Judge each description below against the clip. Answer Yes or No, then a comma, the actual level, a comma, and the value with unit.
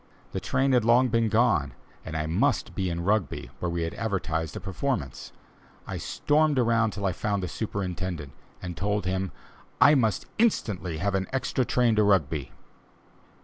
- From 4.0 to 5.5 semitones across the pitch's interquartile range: Yes, average, 5.0 semitones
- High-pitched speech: No, low, 100 Hz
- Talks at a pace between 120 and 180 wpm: Yes, average, 170 wpm